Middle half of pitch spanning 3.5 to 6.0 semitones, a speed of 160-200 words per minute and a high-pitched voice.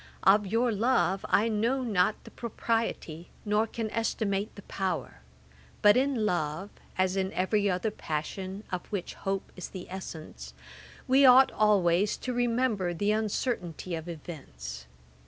No: average, 4.0 semitones; average, 140 wpm; high, 200 Hz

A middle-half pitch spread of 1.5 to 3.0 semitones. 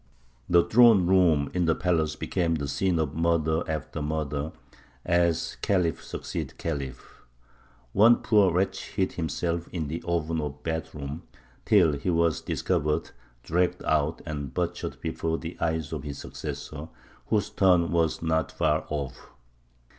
Yes: narrow, 2.4 semitones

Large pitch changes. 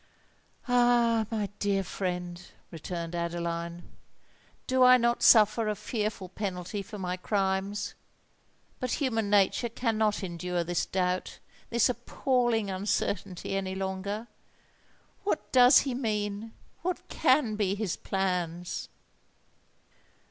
No: average, 4.1 semitones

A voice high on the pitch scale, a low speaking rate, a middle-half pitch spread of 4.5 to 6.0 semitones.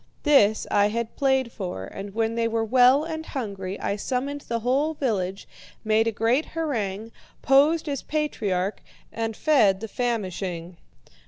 No: high, 230 Hz; average, 150 wpm; average, 5.2 semitones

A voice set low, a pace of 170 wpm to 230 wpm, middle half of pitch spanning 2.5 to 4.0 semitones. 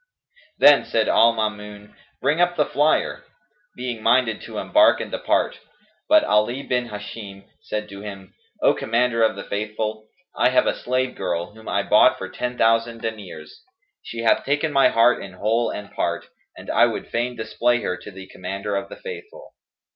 Yes: low, 115 Hz; average, 175 wpm; average, 3.2 semitones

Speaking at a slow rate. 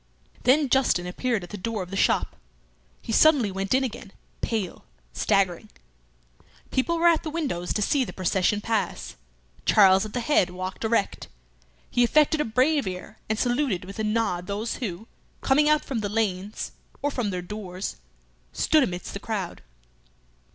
No: average, 165 wpm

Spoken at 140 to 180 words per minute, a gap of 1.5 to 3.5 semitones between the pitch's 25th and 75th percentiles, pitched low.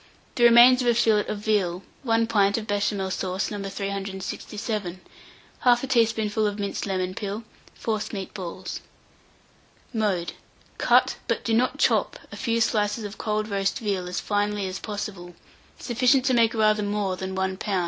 No: average, 160 wpm; average, 2.7 semitones; high, 210 Hz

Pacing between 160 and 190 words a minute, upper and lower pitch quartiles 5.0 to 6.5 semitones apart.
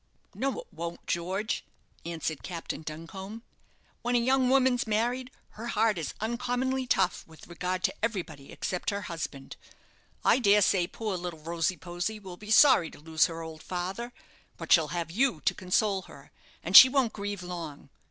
Yes: average, 170 wpm; wide, 5.5 semitones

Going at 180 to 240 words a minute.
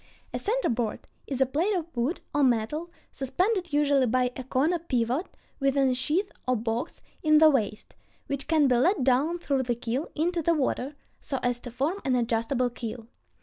Yes: average, 190 wpm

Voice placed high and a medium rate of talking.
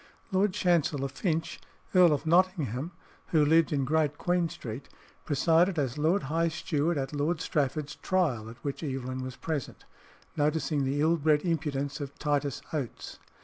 No: medium, 150 Hz; average, 150 wpm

